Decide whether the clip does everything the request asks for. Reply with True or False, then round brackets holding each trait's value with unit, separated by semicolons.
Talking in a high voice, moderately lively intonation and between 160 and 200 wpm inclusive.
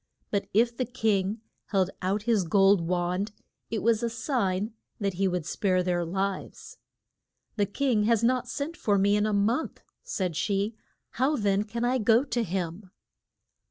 True (205 Hz; 3.5 semitones; 165 wpm)